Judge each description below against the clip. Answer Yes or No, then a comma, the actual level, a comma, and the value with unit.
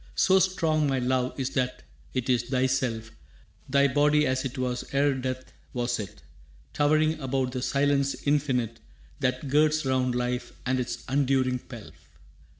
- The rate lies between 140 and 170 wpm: Yes, average, 150 wpm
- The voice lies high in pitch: No, low, 130 Hz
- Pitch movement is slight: Yes, narrow, 2.2 semitones